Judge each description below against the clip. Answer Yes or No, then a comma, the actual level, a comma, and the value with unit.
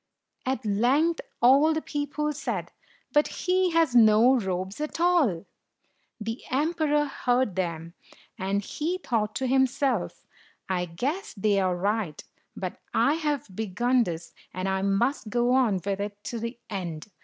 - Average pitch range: No, wide, 6.8 semitones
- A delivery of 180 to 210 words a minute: No, average, 155 wpm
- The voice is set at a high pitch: Yes, high, 240 Hz